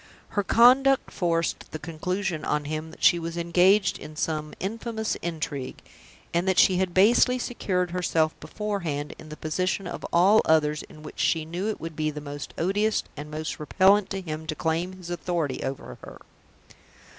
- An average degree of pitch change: Yes, average, 3.7 semitones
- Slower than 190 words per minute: Yes, average, 170 wpm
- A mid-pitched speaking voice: Yes, medium, 170 Hz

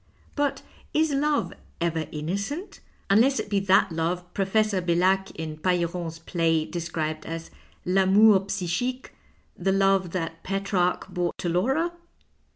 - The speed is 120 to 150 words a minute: Yes, average, 140 wpm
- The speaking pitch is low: No, medium, 185 Hz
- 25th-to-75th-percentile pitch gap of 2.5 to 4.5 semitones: Yes, average, 3.3 semitones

